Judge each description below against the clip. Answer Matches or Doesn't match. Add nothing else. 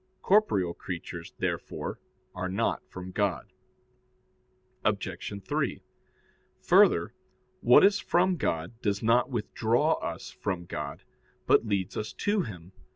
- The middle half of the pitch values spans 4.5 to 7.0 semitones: Matches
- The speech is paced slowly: Matches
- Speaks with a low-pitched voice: Matches